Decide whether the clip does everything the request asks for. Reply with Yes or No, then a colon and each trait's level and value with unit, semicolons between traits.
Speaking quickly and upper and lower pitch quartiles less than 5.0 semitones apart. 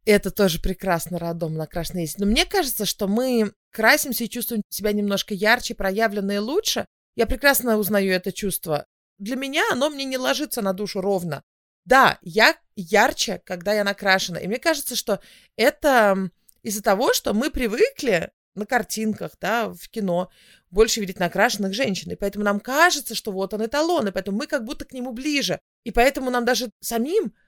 Yes: fast, 170 wpm; average, 4.6 semitones